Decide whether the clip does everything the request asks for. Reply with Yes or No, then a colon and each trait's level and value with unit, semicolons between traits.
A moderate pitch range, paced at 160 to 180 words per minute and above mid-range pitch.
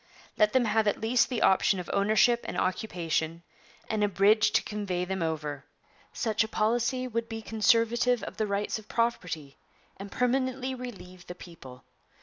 Yes: average, 4.5 semitones; average, 165 wpm; high, 215 Hz